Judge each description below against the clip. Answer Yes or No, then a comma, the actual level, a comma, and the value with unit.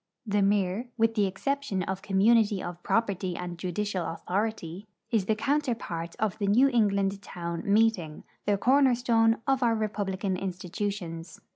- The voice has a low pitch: No, high, 205 Hz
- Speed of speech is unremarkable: Yes, average, 145 wpm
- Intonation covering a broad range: No, average, 3.5 semitones